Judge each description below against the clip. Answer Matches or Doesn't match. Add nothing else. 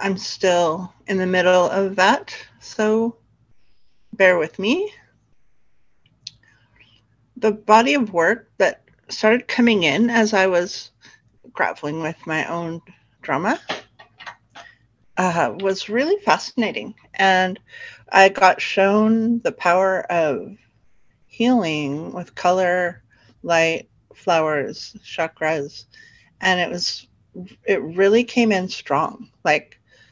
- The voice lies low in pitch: Doesn't match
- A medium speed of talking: Doesn't match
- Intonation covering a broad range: Doesn't match